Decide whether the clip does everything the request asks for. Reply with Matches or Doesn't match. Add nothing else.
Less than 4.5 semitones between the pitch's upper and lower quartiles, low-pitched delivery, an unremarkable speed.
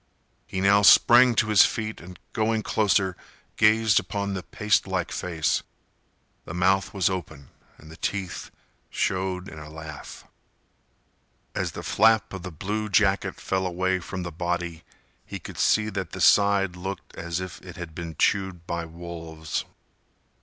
Matches